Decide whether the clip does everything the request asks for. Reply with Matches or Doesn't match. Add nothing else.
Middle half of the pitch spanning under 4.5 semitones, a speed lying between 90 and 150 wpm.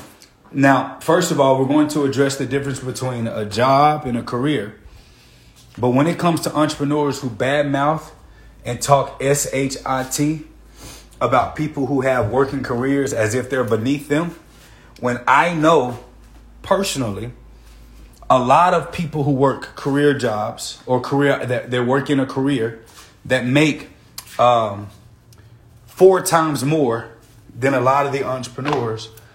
Matches